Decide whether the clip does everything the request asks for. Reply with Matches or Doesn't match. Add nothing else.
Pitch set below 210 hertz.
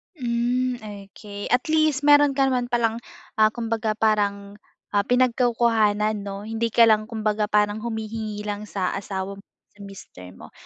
Doesn't match